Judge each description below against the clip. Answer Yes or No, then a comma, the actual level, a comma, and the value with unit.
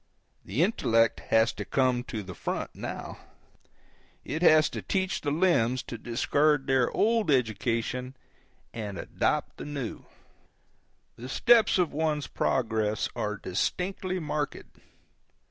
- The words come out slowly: Yes, slow, 125 wpm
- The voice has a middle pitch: No, low, 130 Hz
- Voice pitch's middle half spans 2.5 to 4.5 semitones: No, wide, 5.4 semitones